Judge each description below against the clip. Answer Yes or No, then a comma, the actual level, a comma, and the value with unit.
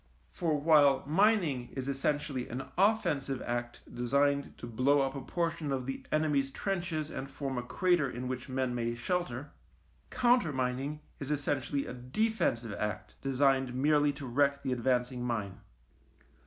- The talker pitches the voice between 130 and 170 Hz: Yes, low, 135 Hz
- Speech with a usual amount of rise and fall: Yes, average, 3.1 semitones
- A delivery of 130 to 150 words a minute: Yes, average, 145 wpm